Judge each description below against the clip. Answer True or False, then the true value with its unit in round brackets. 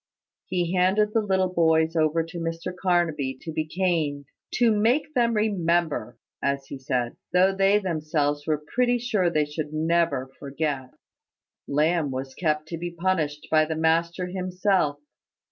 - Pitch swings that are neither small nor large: True (3.7 semitones)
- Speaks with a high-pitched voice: False (165 Hz)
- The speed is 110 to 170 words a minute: True (150 wpm)